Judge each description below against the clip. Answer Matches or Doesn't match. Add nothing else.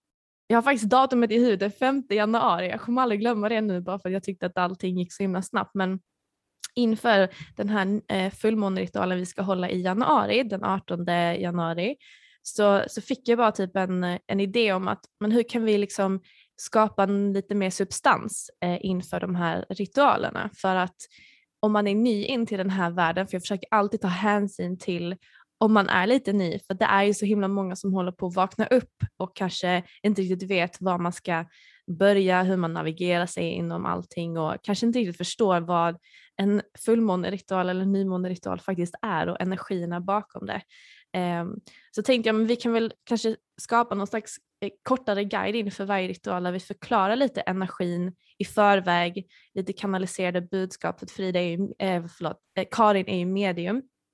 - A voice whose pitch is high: Matches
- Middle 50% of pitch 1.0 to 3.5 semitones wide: Matches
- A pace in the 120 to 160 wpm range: Doesn't match